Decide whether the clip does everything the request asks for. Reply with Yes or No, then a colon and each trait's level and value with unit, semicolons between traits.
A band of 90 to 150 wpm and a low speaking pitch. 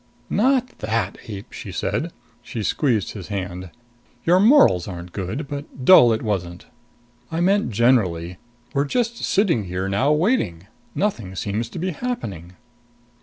Yes: average, 140 wpm; low, 115 Hz